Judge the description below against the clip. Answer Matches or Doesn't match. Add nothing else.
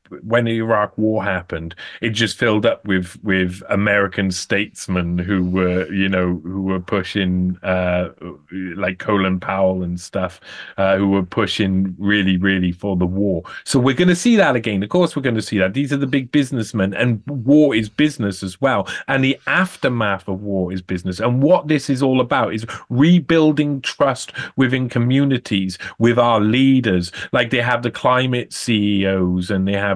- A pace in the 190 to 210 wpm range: Doesn't match